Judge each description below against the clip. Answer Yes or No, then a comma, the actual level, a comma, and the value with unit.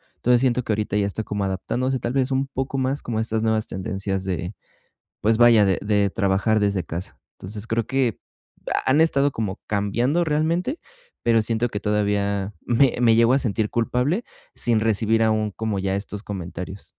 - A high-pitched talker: No, low, 110 Hz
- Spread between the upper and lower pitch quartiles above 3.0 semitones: Yes, average, 3.6 semitones